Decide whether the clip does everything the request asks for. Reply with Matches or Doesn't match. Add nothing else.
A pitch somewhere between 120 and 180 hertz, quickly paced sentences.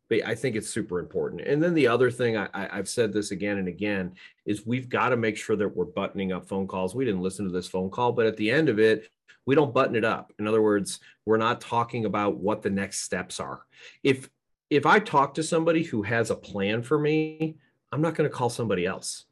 Doesn't match